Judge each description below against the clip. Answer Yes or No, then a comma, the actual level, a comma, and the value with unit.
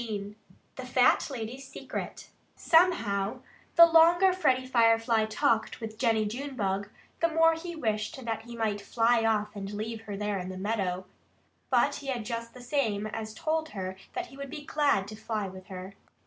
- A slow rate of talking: No, average, 175 wpm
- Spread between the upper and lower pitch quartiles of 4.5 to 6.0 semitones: Yes, average, 4.8 semitones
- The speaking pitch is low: No, high, 225 Hz